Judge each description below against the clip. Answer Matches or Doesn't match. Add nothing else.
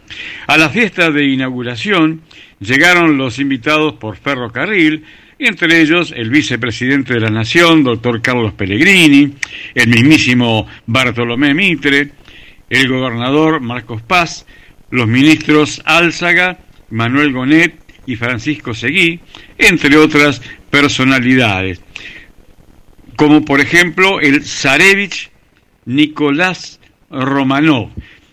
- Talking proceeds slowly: Matches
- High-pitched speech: Doesn't match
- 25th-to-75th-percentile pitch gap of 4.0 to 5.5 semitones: Matches